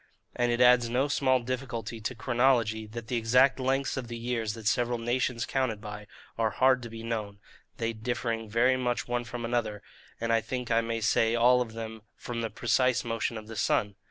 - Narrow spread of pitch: Yes, narrow, 1.8 semitones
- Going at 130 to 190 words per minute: No, fast, 205 wpm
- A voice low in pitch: Yes, low, 115 Hz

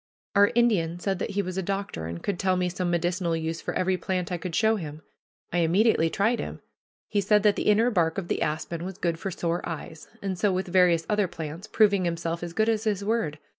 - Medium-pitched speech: Yes, medium, 180 Hz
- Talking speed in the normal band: No, fast, 235 wpm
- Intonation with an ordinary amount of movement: Yes, average, 3.2 semitones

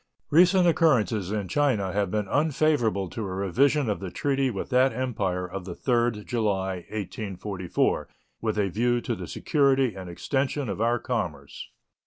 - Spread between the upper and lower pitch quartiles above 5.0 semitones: Yes, wide, 5.5 semitones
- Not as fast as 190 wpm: Yes, average, 160 wpm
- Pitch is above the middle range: No, low, 110 Hz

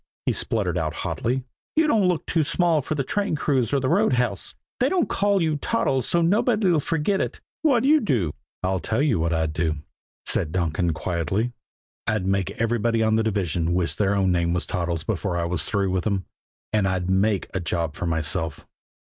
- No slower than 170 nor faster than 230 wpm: Yes, average, 200 wpm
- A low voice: Yes, low, 100 Hz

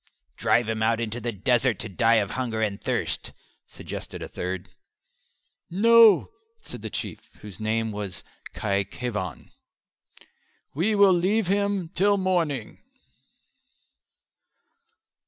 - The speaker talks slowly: Yes, slow, 120 wpm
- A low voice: Yes, low, 120 Hz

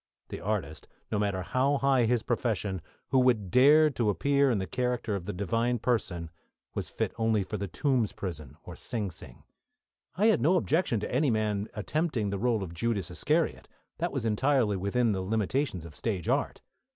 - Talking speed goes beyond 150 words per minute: Yes, average, 190 wpm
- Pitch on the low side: Yes, low, 110 Hz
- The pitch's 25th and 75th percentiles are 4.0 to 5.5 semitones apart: Yes, average, 4.7 semitones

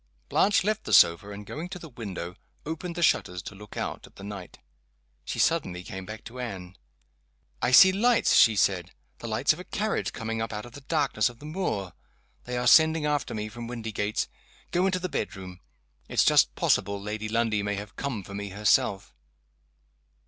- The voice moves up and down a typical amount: No, wide, 6.8 semitones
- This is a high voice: No, low, 110 Hz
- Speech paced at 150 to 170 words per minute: No, average, 195 wpm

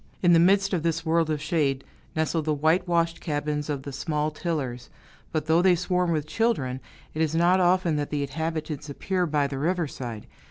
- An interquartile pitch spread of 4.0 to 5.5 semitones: No, average, 2.9 semitones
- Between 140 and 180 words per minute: No, average, 190 wpm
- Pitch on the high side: No, medium, 160 Hz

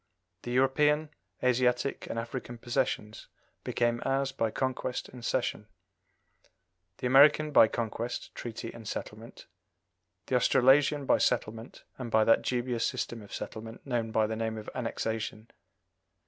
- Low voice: Yes, low, 120 Hz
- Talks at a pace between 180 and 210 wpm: No, slow, 135 wpm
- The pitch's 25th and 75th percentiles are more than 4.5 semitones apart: No, narrow, 2.6 semitones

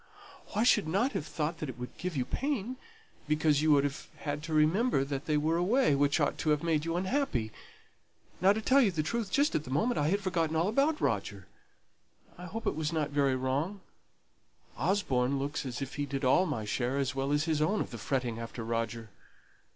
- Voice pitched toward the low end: No, medium, 150 Hz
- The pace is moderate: No, fast, 210 wpm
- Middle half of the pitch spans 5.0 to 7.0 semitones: Yes, wide, 5.6 semitones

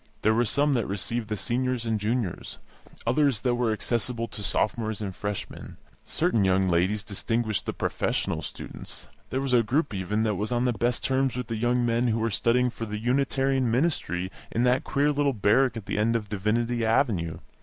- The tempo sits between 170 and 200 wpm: Yes, average, 195 wpm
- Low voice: Yes, low, 115 Hz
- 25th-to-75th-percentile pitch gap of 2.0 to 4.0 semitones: Yes, average, 2.9 semitones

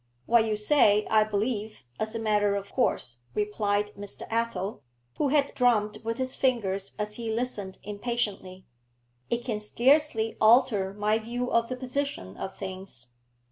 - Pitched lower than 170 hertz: No, high, 215 Hz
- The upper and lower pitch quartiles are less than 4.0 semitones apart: Yes, average, 2.9 semitones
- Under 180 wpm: Yes, average, 150 wpm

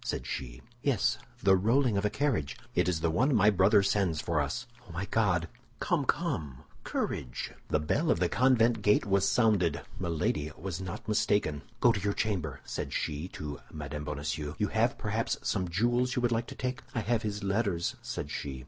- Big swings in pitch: Yes, wide, 6.3 semitones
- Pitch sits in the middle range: No, very low, 95 Hz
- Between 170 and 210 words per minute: Yes, average, 195 wpm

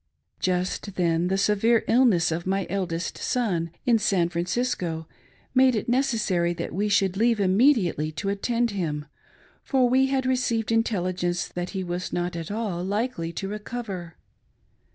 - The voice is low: No, high, 195 Hz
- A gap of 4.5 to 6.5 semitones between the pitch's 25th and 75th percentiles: Yes, average, 4.8 semitones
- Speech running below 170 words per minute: Yes, average, 150 wpm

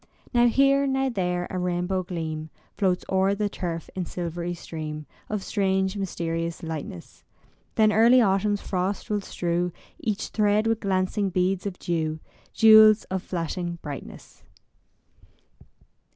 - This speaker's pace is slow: Yes, slow, 130 wpm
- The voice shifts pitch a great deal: No, average, 3.4 semitones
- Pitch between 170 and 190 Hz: Yes, medium, 185 Hz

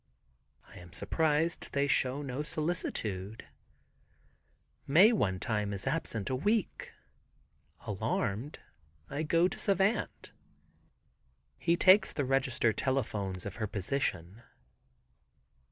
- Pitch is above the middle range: No, low, 135 Hz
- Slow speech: Yes, slow, 105 wpm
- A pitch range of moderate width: No, wide, 7.6 semitones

